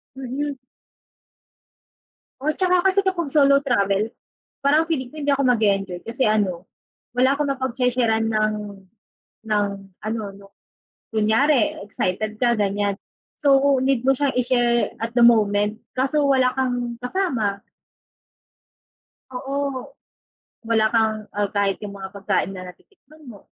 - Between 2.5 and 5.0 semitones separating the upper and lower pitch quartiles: Yes, average, 4.4 semitones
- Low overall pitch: No, high, 240 Hz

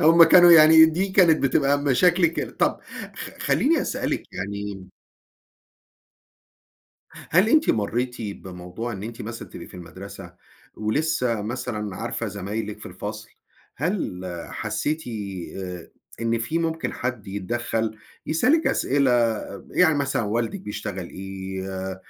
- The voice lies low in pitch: Yes, low, 115 Hz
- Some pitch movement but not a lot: No, wide, 7.7 semitones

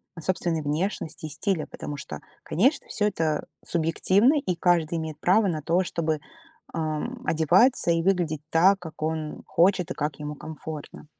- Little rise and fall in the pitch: No, average, 3.0 semitones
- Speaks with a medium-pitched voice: Yes, medium, 165 Hz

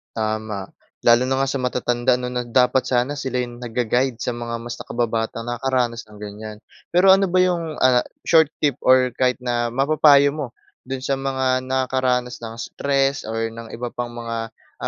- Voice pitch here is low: Yes, low, 125 Hz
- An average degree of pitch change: No, narrow, 2.2 semitones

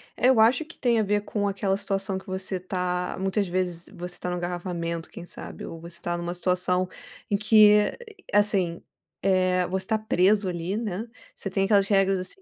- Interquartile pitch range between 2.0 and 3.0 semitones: Yes, narrow, 2.5 semitones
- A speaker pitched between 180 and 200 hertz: Yes, high, 190 Hz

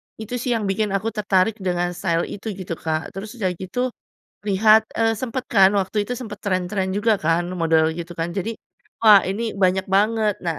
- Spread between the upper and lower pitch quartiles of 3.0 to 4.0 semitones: Yes, average, 3.3 semitones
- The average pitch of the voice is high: Yes, high, 195 Hz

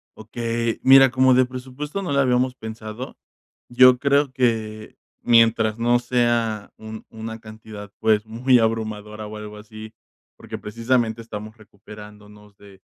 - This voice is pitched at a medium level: No, low, 115 Hz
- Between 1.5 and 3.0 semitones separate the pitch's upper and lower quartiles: Yes, narrow, 2.6 semitones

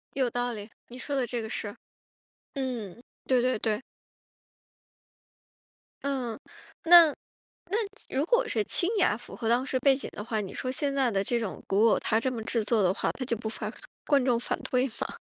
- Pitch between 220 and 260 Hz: Yes, high, 245 Hz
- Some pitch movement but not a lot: Yes, average, 3.3 semitones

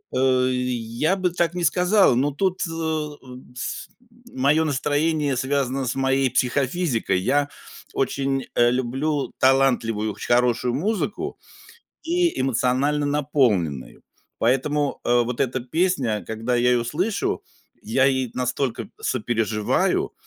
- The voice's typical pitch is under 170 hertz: Yes, low, 135 Hz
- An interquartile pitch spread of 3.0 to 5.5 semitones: Yes, average, 3.5 semitones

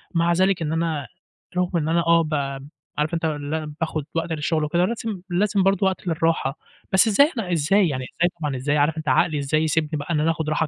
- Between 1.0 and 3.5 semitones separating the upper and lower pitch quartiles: Yes, average, 2.7 semitones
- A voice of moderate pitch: Yes, medium, 165 Hz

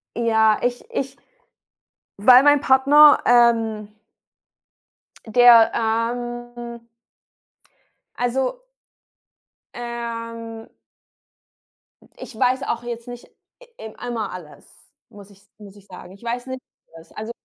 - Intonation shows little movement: Yes, narrow, 1.8 semitones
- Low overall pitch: No, high, 235 Hz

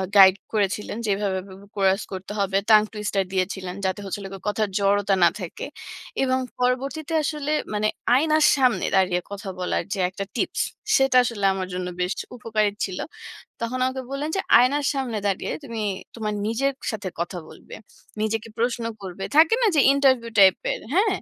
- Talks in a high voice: Yes, high, 210 Hz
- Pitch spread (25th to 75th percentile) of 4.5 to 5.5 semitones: Yes, average, 5.0 semitones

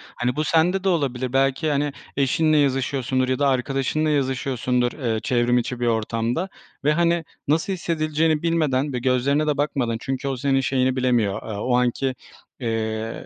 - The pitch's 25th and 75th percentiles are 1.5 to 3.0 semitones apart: No, average, 3.5 semitones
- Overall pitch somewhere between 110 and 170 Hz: Yes, low, 135 Hz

